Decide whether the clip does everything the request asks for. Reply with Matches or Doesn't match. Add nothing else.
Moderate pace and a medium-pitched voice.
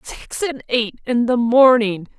Doesn't match